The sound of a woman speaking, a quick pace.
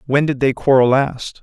No: male; fast, 210 wpm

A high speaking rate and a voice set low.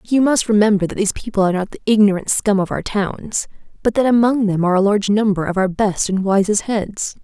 No: fast, 230 wpm; high, 205 Hz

